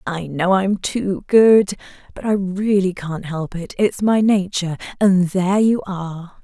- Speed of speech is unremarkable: Yes, average, 160 wpm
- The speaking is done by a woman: Yes, female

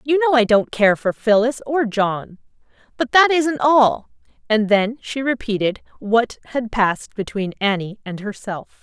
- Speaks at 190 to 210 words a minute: No, average, 165 wpm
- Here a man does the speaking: No, female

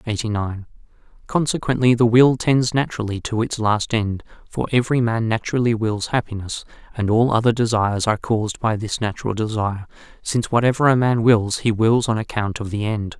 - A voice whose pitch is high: No, low, 115 Hz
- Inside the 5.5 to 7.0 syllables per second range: Yes, 5.7 syllables/s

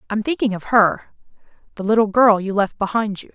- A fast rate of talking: No, average, 180 wpm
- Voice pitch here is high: Yes, high, 210 Hz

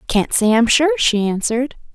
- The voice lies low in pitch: No, high, 235 Hz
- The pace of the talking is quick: No, average, 185 wpm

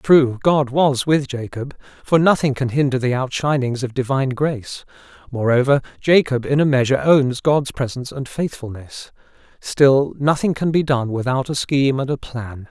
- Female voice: No, male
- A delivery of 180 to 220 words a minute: No, average, 160 wpm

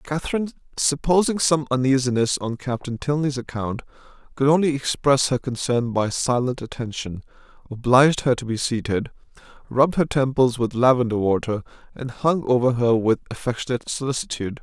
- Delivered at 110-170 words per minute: Yes, average, 140 wpm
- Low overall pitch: Yes, low, 130 Hz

